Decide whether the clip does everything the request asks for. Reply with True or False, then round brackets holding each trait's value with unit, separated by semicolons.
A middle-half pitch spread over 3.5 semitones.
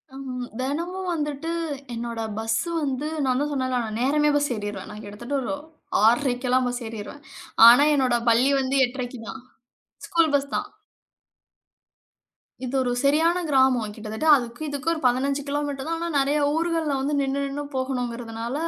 False (3.1 semitones)